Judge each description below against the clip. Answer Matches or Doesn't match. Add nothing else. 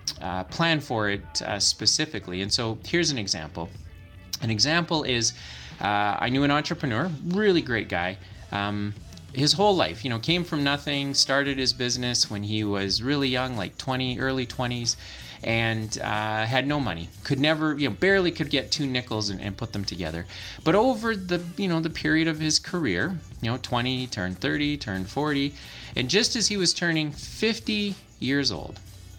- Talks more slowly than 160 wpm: Doesn't match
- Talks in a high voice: Doesn't match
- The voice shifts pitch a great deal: Matches